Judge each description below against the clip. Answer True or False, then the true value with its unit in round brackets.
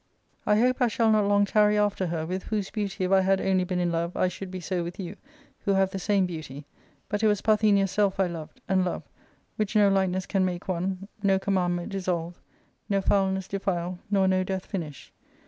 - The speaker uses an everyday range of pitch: False (2.0 semitones)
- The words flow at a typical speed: False (225 wpm)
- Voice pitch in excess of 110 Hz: True (190 Hz)